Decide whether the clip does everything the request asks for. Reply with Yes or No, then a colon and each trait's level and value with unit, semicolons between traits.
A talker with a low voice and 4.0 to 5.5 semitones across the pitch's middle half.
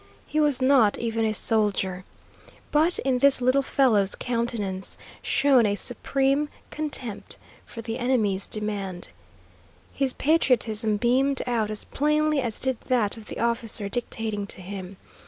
No: high, 235 Hz; average, 4.3 semitones